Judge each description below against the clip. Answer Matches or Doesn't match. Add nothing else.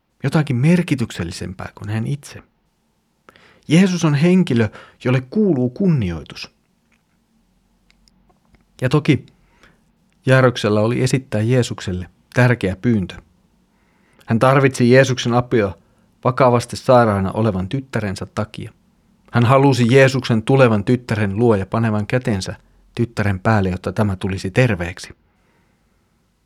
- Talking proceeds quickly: Doesn't match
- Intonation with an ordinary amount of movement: Matches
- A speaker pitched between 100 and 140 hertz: Matches